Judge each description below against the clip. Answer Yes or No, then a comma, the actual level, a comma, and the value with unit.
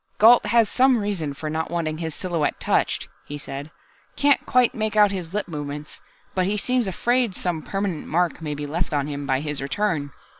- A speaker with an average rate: Yes, average, 195 wpm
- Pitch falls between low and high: Yes, medium, 175 Hz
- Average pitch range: No, wide, 5.9 semitones